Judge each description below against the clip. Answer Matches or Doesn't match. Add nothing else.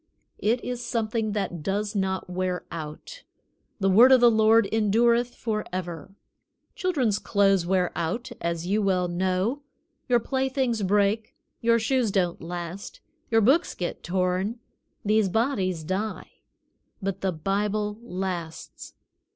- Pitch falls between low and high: Doesn't match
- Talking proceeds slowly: Matches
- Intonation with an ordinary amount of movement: Matches